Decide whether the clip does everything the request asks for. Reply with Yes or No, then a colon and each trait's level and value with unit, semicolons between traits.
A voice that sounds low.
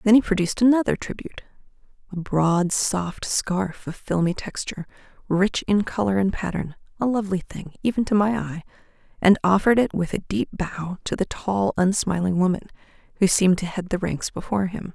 No: high, 190 Hz